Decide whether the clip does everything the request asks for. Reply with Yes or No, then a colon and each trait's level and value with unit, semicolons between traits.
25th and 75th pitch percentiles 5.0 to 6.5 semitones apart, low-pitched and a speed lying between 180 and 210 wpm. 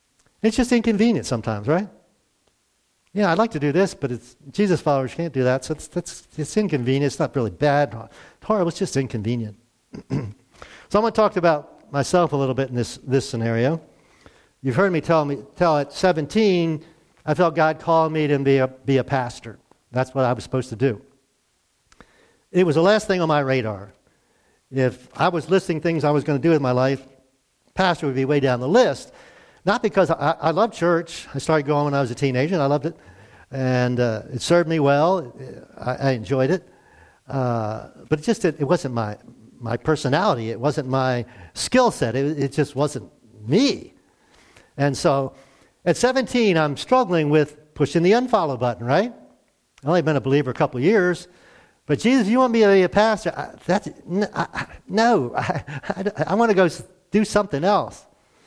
No: wide, 5.5 semitones; medium, 150 Hz; average, 200 wpm